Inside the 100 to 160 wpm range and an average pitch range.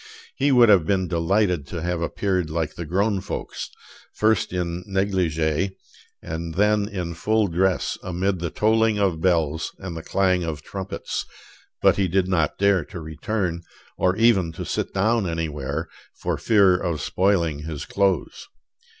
Yes: average, 155 wpm; average, 3.2 semitones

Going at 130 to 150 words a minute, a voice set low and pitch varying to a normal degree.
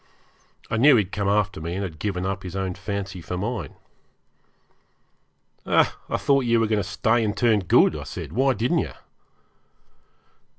No: average, 175 wpm; low, 100 Hz; average, 3.4 semitones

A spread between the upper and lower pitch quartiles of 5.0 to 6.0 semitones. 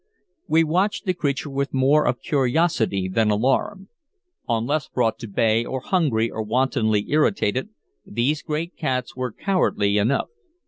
Yes: wide, 5.5 semitones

